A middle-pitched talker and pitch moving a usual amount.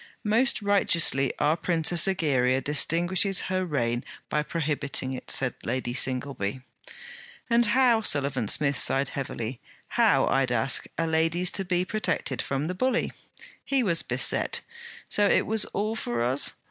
No: medium, 155 Hz; wide, 6.5 semitones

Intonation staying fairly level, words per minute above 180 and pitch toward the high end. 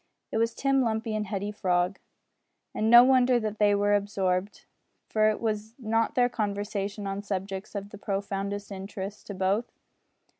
No: narrow, 2.0 semitones; average, 155 wpm; high, 205 Hz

